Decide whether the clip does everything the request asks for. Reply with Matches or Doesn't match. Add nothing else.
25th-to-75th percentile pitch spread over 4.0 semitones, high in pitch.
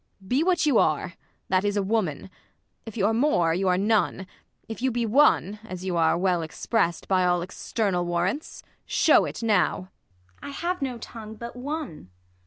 Matches